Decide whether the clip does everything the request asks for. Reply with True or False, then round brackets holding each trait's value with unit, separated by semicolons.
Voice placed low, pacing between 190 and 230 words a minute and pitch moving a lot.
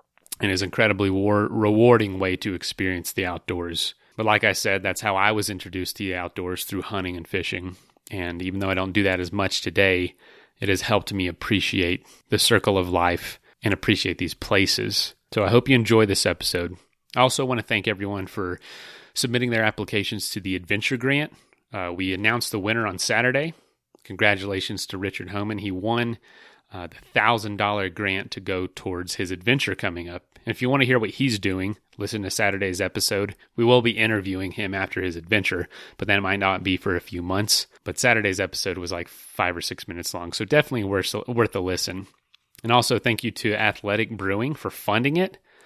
False (100 Hz; 200 wpm; 3.2 semitones)